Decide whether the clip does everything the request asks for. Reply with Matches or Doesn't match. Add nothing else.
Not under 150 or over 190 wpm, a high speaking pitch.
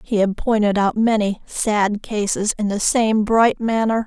Matches